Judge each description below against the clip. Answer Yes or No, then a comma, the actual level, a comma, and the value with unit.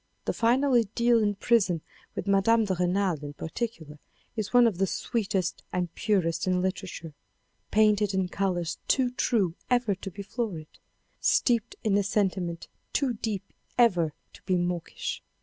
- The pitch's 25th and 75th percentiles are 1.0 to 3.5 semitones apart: No, average, 4.3 semitones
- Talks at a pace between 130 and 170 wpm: Yes, average, 150 wpm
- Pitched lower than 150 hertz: No, high, 195 Hz